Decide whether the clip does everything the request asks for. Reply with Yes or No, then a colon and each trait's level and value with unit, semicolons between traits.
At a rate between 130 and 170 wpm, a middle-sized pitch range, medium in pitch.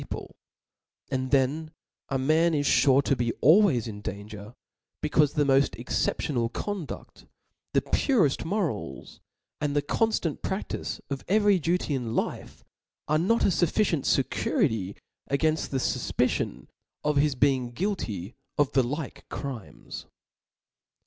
Yes: average, 140 wpm; average, 4.5 semitones; medium, 145 Hz